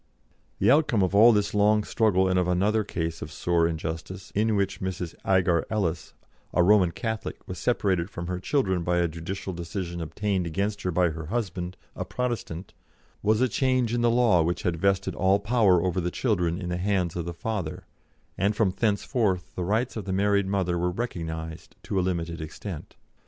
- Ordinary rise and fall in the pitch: Yes, average, 3.4 semitones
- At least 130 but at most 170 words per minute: No, average, 190 wpm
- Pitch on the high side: No, very low, 95 Hz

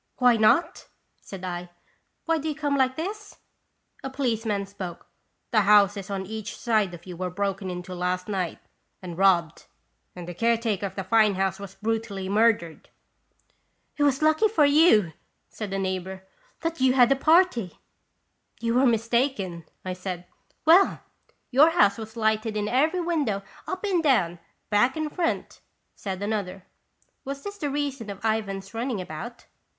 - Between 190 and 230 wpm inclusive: No, average, 165 wpm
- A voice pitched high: Yes, high, 220 Hz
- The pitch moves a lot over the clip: Yes, wide, 6.2 semitones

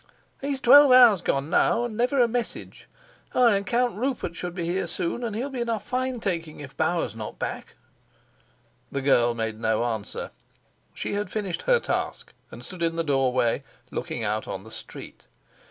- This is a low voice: No, medium, 185 Hz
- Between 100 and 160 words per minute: No, average, 185 wpm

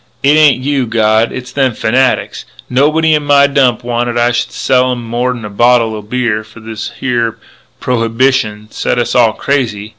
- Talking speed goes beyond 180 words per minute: No, average, 175 wpm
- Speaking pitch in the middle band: No, low, 120 Hz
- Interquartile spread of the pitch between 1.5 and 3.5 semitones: Yes, average, 2.7 semitones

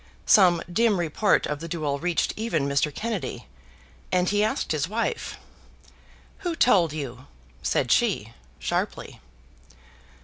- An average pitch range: No, wide, 6.0 semitones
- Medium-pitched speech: Yes, medium, 175 Hz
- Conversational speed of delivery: No, slow, 125 wpm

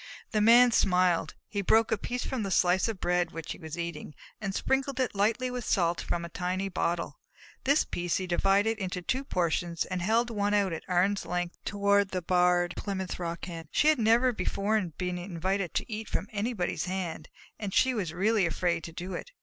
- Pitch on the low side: No, high, 190 Hz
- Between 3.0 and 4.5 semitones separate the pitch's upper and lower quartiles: Yes, average, 3.7 semitones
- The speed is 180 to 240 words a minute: Yes, average, 200 wpm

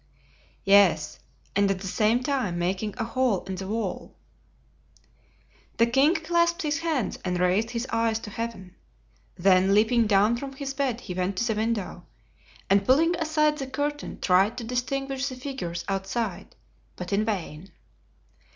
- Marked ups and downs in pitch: Yes, wide, 5.7 semitones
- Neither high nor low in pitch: No, high, 225 Hz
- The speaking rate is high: No, average, 155 wpm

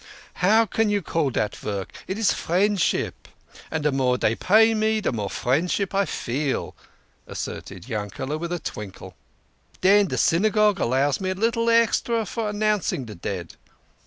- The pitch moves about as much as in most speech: No, wide, 8.8 semitones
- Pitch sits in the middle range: Yes, medium, 180 Hz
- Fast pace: No, average, 160 wpm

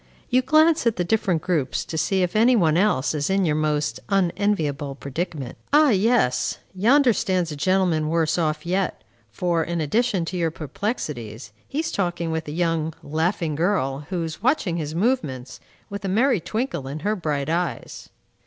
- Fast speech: No, average, 175 wpm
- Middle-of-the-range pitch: Yes, medium, 170 Hz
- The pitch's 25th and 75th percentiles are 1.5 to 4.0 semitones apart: No, average, 4.9 semitones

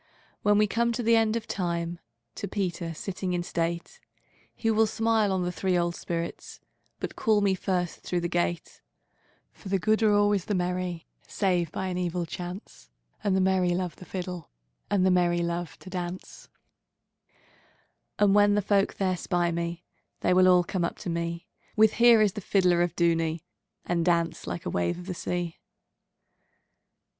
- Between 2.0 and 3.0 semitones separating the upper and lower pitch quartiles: Yes, narrow, 2.6 semitones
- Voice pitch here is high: No, medium, 180 Hz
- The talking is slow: No, average, 155 wpm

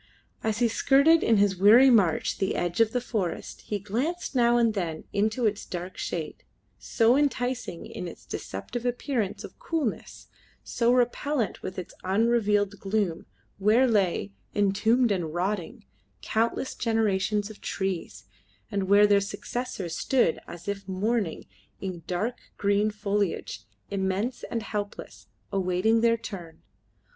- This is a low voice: No, high, 210 Hz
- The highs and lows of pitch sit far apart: No, average, 3.6 semitones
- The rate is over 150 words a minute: No, slow, 135 wpm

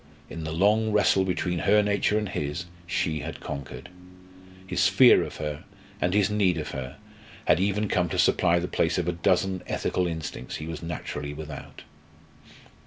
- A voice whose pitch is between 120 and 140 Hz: No, very low, 90 Hz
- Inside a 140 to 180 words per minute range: Yes, average, 175 wpm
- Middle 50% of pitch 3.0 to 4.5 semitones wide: Yes, average, 3.6 semitones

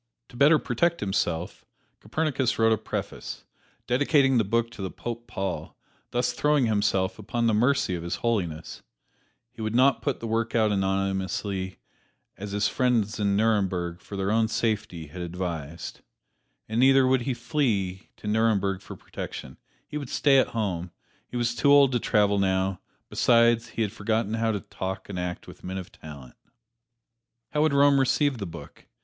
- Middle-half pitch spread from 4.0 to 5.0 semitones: Yes, average, 4.3 semitones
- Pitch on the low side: Yes, low, 110 Hz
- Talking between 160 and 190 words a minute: Yes, average, 170 wpm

